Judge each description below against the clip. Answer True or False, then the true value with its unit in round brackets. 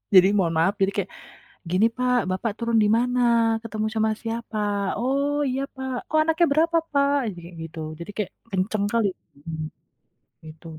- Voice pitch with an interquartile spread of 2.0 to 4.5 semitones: False (5.6 semitones)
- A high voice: True (220 Hz)